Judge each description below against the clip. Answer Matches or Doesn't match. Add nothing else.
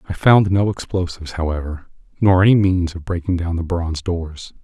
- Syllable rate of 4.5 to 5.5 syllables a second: Matches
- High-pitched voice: Doesn't match